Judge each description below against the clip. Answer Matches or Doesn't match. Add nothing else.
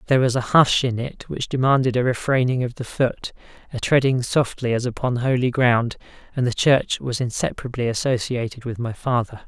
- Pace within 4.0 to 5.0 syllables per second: Doesn't match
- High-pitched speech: Doesn't match